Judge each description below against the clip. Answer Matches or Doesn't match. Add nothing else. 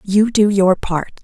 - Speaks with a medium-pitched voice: Doesn't match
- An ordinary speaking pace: Matches